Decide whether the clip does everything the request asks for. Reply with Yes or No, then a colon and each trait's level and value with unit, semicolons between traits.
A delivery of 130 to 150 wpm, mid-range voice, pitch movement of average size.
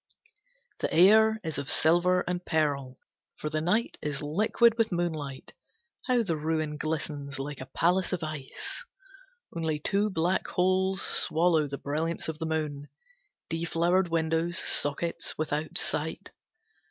Yes: average, 140 wpm; medium, 160 Hz; average, 3.1 semitones